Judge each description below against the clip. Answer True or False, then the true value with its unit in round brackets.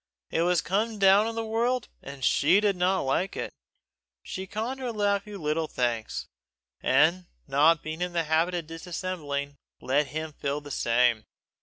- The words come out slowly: False (170 wpm)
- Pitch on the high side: False (170 Hz)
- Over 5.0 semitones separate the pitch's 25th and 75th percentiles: True (5.6 semitones)